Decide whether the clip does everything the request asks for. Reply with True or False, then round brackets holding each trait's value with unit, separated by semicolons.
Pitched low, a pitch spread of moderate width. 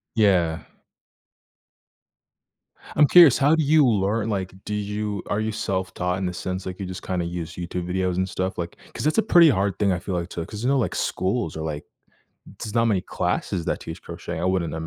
True (95 Hz; 3.4 semitones)